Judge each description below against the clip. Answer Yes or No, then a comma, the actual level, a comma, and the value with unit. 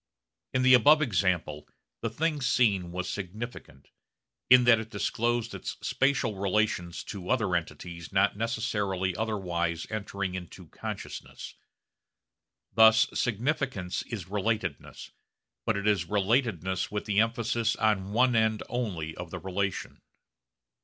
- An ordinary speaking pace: No, slow, 125 wpm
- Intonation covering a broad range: No, average, 4.1 semitones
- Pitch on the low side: Yes, low, 105 Hz